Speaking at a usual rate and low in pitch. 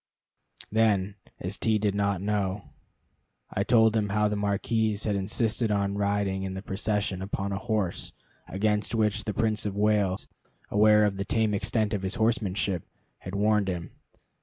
Yes: average, 160 wpm; low, 105 Hz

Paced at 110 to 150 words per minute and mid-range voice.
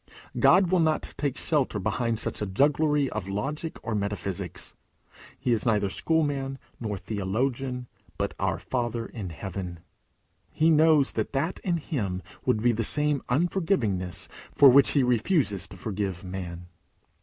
No: average, 145 wpm; low, 120 Hz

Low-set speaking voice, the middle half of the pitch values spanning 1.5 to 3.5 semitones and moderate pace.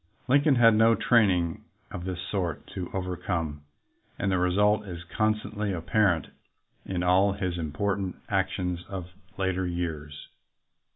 No: very low, 95 Hz; average, 2.8 semitones; slow, 130 wpm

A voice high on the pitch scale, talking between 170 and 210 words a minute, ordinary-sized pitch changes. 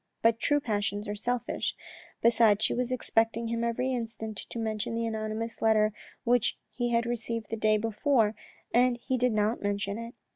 No: high, 230 Hz; average, 175 wpm; narrow, 1.8 semitones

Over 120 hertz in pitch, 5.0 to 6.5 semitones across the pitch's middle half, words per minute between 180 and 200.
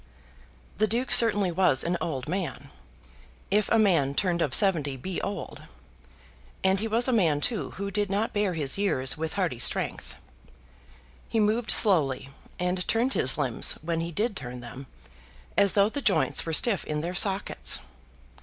No: medium, 185 Hz; wide, 5.4 semitones; average, 165 wpm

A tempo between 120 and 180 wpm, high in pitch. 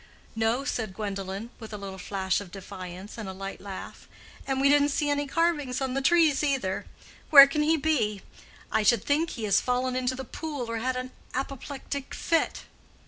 No: average, 190 wpm; very high, 255 Hz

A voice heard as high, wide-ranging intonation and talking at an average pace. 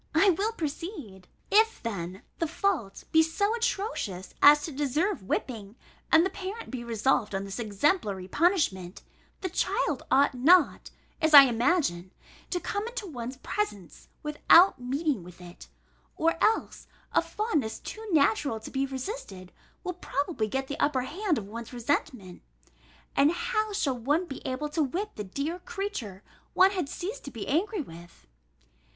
Yes: very high, 285 Hz; wide, 8.6 semitones; average, 155 wpm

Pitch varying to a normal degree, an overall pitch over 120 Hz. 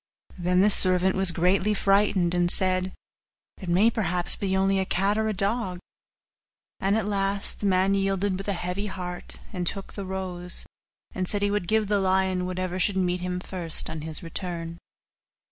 No: narrow, 1.7 semitones; high, 190 Hz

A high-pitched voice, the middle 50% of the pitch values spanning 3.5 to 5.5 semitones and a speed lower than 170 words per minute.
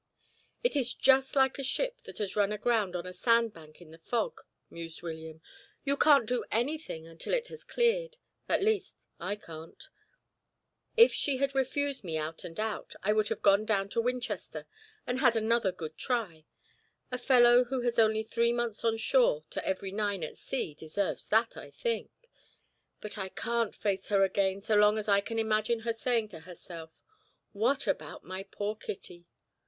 No: high, 215 Hz; average, 4.8 semitones; average, 180 wpm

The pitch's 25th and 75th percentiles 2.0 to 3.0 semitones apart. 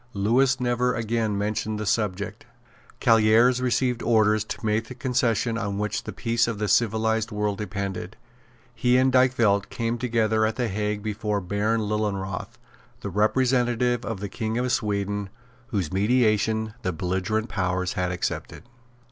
Yes: narrow, 2.5 semitones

